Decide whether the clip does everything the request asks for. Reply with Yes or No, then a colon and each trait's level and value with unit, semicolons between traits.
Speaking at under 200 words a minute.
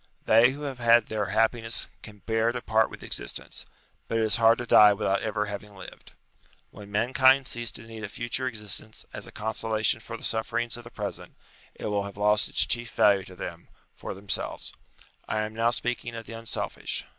No: fast, 205 wpm